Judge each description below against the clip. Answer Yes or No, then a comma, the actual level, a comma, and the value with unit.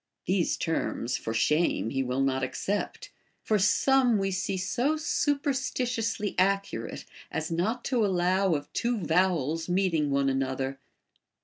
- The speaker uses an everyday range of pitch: No, wide, 7.6 semitones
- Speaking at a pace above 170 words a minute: No, slow, 135 wpm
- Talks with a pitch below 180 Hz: No, medium, 185 Hz